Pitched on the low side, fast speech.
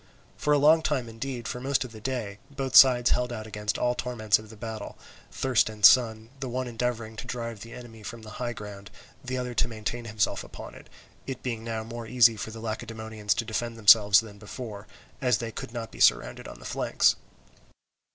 Yes: low, 115 Hz; fast, 210 wpm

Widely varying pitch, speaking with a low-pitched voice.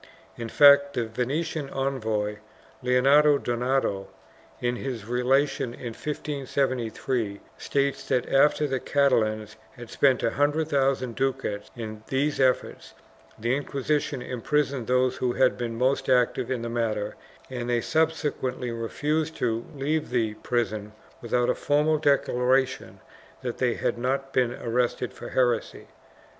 No: average, 2.9 semitones; low, 125 Hz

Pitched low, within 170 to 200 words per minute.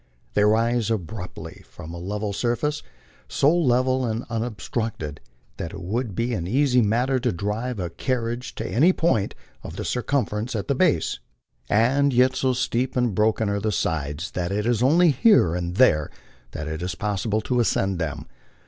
Yes: low, 115 Hz; average, 180 wpm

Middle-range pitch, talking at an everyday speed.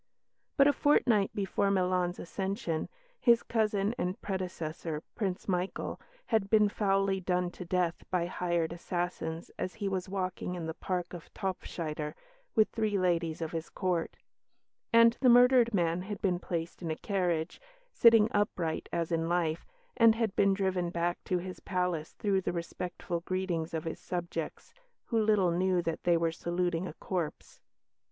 Yes: medium, 180 Hz; average, 160 wpm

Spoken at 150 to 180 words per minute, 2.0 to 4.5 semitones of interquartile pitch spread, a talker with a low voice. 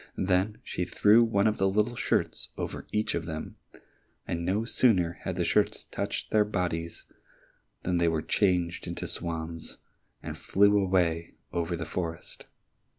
Yes: average, 155 wpm; average, 3.5 semitones; very low, 90 Hz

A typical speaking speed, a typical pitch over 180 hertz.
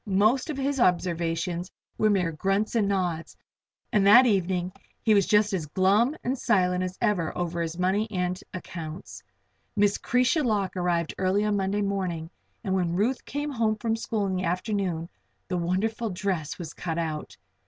Yes: average, 170 wpm; high, 190 Hz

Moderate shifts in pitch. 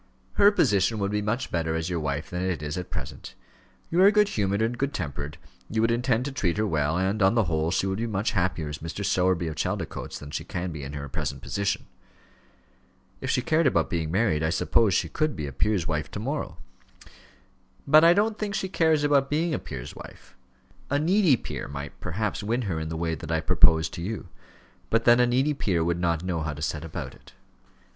No: wide, 7.2 semitones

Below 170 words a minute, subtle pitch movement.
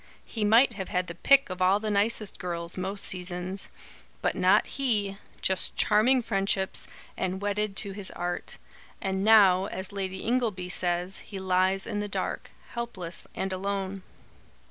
Yes: average, 155 wpm; narrow, 2.1 semitones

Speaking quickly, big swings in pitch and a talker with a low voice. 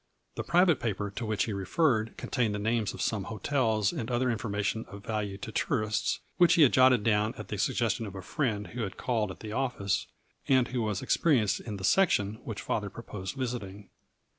No: fast, 210 wpm; average, 3.4 semitones; low, 110 Hz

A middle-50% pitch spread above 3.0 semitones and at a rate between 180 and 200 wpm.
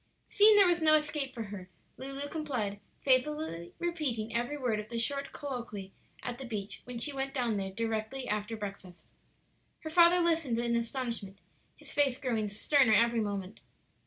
No: average, 5.1 semitones; average, 165 wpm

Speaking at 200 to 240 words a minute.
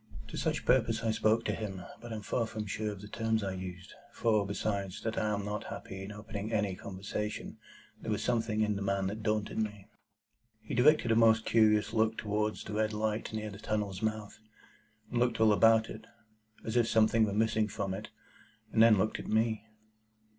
Yes: fast, 205 wpm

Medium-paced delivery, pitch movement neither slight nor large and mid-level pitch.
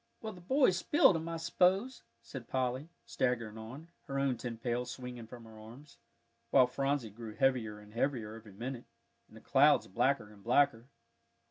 No: average, 170 wpm; average, 4.1 semitones; low, 125 Hz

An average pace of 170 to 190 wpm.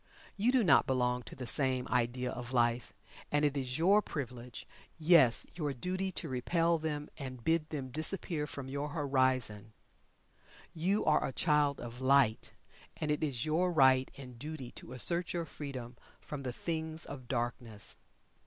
No: average, 160 wpm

